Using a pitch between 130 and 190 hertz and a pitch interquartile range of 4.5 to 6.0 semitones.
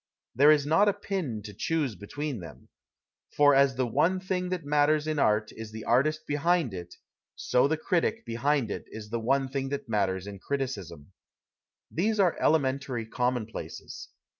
Yes: low, 135 Hz; wide, 5.6 semitones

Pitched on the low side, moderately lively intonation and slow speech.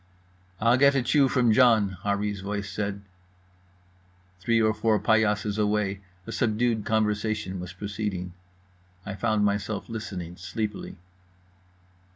No: low, 105 Hz; narrow, 1.8 semitones; slow, 120 wpm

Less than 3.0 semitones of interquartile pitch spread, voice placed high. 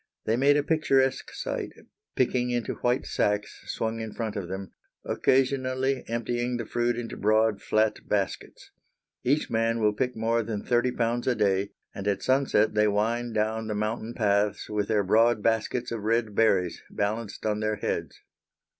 No: narrow, 2.4 semitones; low, 115 Hz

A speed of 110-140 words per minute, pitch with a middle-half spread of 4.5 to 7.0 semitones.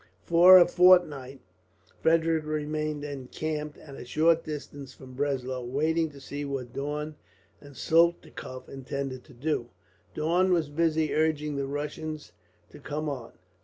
No: slow, 135 wpm; narrow, 2.5 semitones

